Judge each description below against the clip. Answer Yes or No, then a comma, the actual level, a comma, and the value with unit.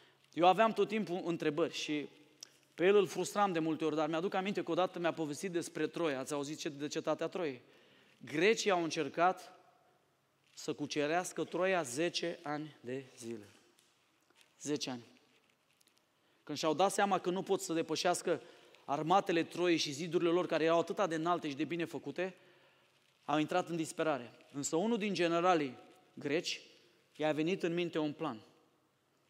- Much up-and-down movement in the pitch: No, average, 2.9 semitones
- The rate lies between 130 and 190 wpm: Yes, average, 160 wpm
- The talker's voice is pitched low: No, medium, 165 Hz